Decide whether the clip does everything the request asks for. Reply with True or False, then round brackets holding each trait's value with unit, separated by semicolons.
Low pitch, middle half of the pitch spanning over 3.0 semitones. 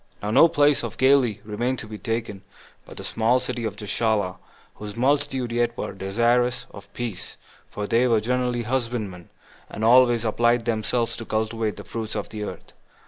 False (115 Hz; 2.5 semitones)